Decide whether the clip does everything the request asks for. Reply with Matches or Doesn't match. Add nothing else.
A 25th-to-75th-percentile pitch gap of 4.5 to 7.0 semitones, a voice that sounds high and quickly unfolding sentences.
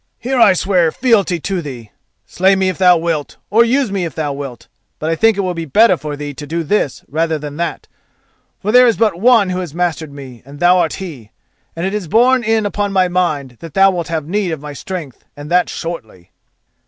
Doesn't match